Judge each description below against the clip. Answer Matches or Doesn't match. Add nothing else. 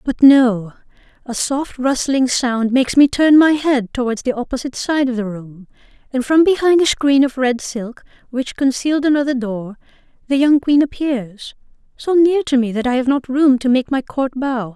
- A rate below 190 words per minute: Doesn't match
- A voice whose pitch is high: Matches